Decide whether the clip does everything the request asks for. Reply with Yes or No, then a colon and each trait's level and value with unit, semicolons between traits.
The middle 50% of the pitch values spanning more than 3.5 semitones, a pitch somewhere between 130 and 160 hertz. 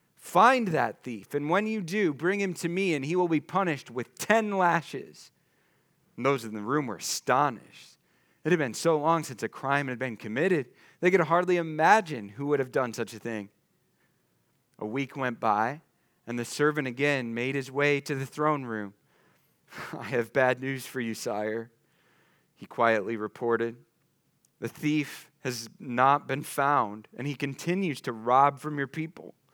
Yes: average, 4.8 semitones; medium, 140 Hz